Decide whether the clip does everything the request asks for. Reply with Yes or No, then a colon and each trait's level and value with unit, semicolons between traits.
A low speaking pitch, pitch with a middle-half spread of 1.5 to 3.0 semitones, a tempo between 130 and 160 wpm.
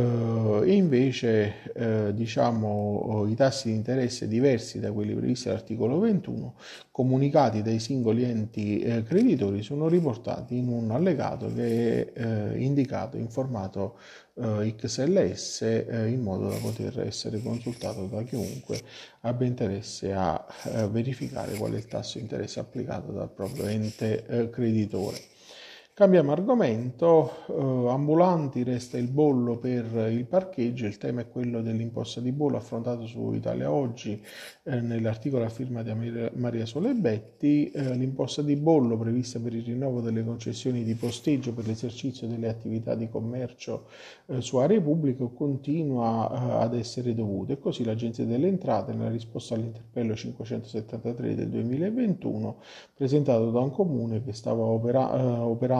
Yes: low, 120 Hz; average, 2.7 semitones; average, 145 wpm